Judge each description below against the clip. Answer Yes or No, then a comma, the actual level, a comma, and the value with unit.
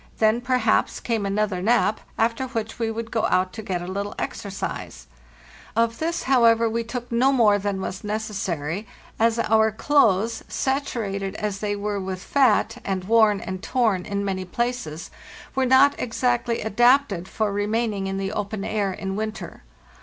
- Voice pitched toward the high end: Yes, high, 215 Hz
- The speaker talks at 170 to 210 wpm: No, average, 160 wpm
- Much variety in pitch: No, average, 3.0 semitones